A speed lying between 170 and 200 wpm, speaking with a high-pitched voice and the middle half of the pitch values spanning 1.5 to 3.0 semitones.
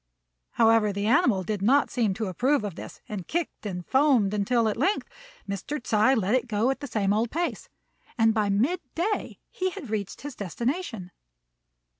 No: average, 180 wpm; high, 225 Hz; average, 4.9 semitones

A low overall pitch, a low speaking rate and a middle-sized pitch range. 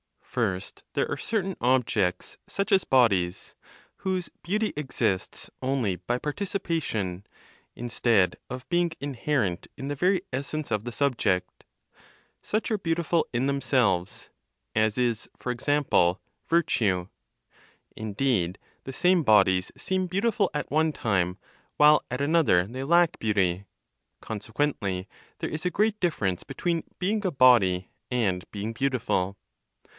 No: low, 130 Hz; slow, 125 wpm; wide, 8.5 semitones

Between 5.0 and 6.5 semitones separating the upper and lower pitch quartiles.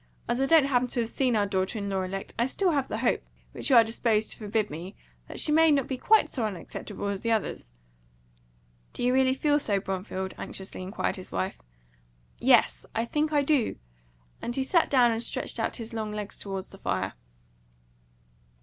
Yes: average, 5.3 semitones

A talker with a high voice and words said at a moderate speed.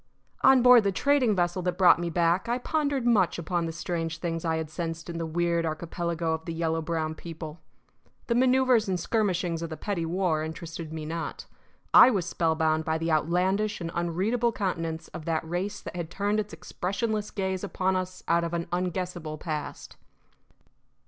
No: medium, 175 Hz; average, 180 wpm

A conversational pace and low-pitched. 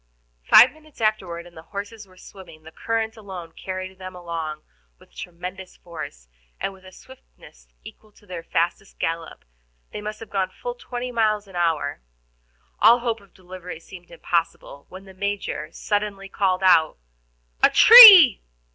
No: average, 155 wpm; high, 190 Hz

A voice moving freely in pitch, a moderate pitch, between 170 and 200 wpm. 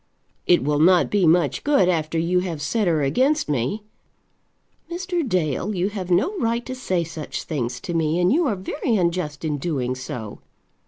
Yes: wide, 5.7 semitones; medium, 175 Hz; average, 180 wpm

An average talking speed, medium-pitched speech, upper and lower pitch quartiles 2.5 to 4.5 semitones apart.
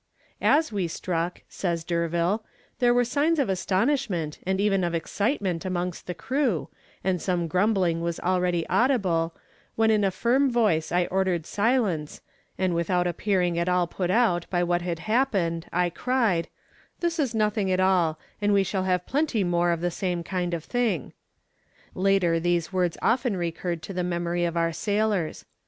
Yes: average, 170 wpm; medium, 180 Hz; average, 3.6 semitones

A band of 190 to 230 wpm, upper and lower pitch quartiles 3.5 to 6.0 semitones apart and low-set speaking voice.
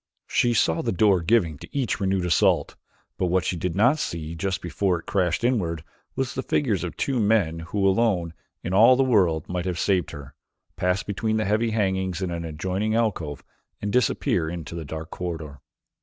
Yes: average, 195 wpm; average, 4.5 semitones; very low, 95 Hz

